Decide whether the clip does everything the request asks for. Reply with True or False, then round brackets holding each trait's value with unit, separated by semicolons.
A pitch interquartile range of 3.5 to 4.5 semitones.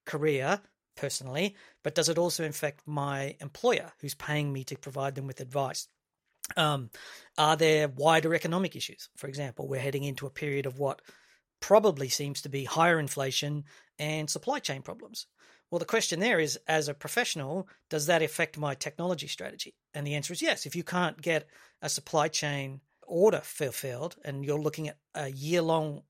False (3.0 semitones)